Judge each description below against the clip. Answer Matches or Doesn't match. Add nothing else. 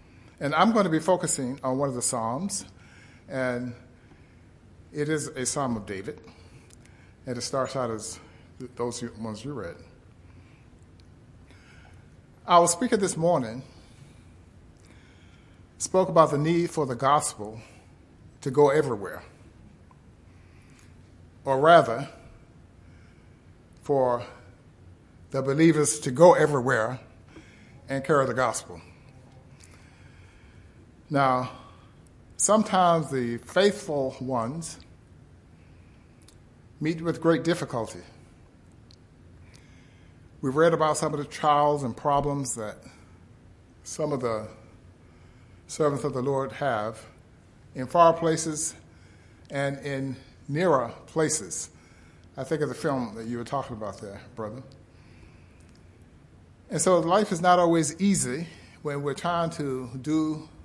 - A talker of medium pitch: Doesn't match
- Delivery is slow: Matches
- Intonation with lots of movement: Matches